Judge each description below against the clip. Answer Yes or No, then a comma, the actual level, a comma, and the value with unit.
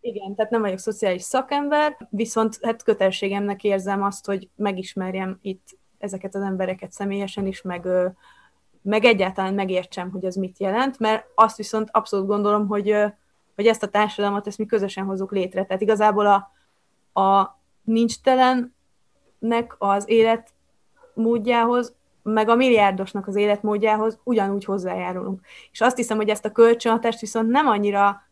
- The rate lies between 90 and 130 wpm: No, average, 140 wpm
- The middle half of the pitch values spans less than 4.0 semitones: Yes, narrow, 2.5 semitones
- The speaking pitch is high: Yes, high, 210 Hz